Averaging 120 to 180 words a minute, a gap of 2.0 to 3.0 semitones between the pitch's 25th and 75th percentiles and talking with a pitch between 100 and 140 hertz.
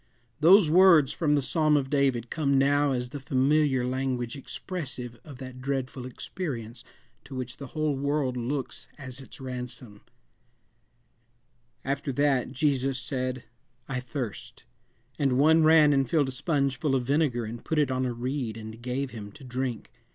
Yes: average, 160 wpm; narrow, 2.6 semitones; low, 135 Hz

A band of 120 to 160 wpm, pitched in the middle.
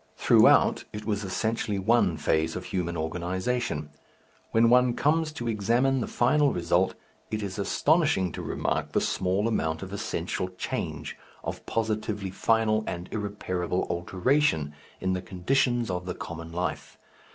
No: average, 140 wpm; low, 100 Hz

